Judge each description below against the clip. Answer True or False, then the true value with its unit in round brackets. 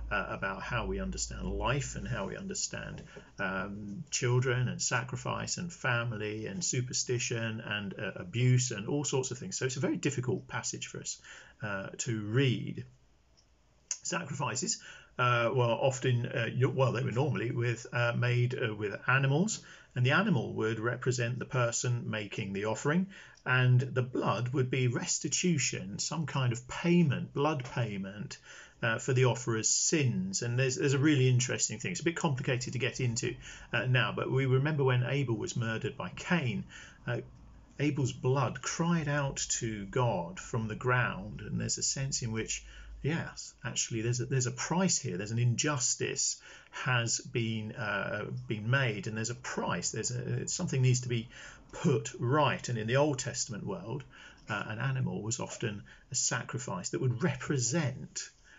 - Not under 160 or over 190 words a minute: True (170 wpm)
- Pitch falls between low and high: False (125 Hz)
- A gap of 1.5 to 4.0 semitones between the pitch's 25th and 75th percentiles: True (3.3 semitones)